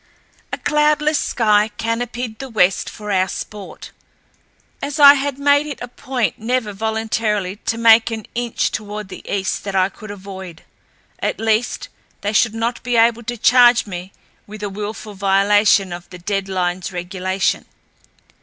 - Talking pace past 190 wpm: No, average, 155 wpm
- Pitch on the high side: Yes, high, 215 Hz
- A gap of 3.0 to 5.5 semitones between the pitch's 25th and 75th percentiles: Yes, average, 3.5 semitones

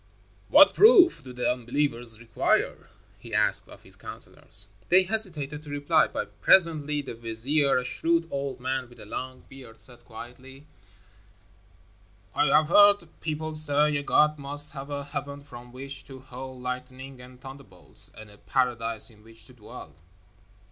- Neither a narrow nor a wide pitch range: Yes, average, 3.3 semitones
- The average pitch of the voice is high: No, low, 135 Hz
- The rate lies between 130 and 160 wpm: Yes, average, 155 wpm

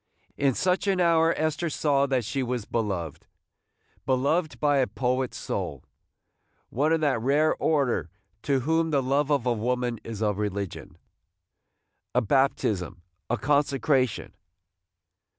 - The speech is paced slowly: No, average, 145 wpm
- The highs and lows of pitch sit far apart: No, average, 4.5 semitones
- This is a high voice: No, low, 135 Hz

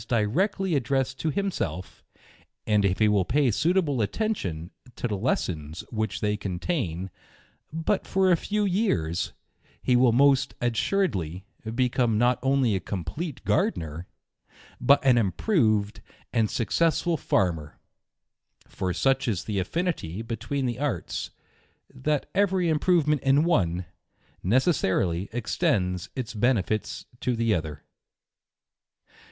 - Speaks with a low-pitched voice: Yes, low, 120 Hz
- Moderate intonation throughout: No, wide, 7.6 semitones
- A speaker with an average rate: No, slow, 120 wpm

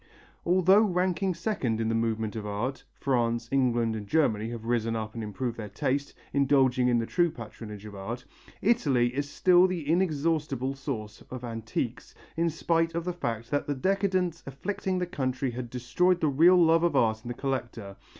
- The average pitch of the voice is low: Yes, low, 130 Hz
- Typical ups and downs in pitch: No, wide, 6.5 semitones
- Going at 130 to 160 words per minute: No, average, 180 wpm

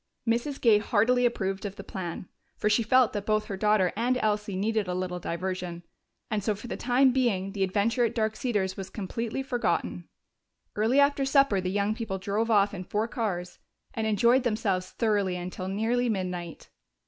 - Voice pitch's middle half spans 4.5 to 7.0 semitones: No, average, 3.6 semitones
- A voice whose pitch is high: Yes, high, 210 Hz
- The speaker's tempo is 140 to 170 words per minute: No, average, 185 wpm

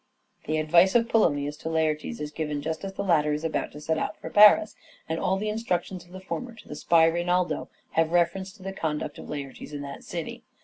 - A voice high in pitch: No, medium, 170 Hz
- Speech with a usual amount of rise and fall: Yes, average, 4.1 semitones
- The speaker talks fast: Yes, fast, 235 wpm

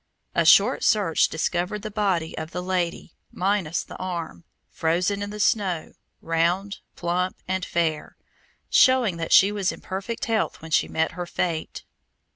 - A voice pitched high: No, medium, 180 Hz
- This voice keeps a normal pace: Yes, average, 155 wpm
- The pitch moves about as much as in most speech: Yes, average, 3.3 semitones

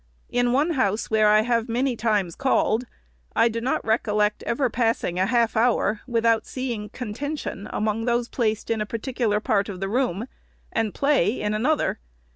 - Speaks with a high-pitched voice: Yes, high, 230 Hz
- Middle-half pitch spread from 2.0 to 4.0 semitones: Yes, average, 2.7 semitones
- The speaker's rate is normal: Yes, average, 170 wpm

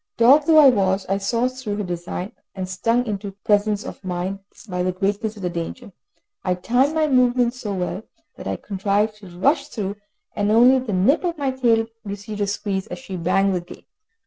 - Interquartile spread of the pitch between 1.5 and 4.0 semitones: No, average, 4.4 semitones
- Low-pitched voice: No, high, 205 Hz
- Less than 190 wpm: No, average, 200 wpm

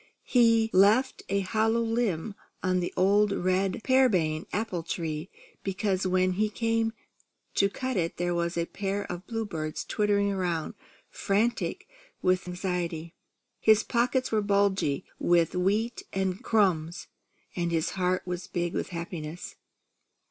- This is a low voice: No, high, 190 Hz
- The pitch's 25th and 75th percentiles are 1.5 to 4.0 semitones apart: Yes, average, 3.6 semitones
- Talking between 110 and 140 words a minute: Yes, slow, 135 wpm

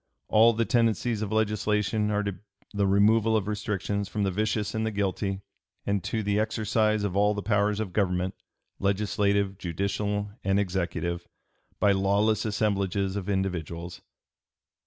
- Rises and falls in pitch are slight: Yes, narrow, 1.7 semitones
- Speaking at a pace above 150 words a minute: No, average, 145 wpm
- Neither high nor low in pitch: No, low, 100 Hz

